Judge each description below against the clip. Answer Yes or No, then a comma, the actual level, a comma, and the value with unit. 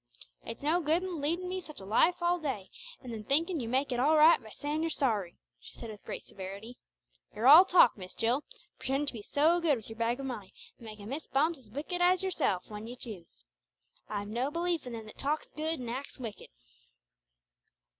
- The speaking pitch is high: Yes, very high, 270 Hz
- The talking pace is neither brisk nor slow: No, fast, 215 wpm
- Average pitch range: No, wide, 6.2 semitones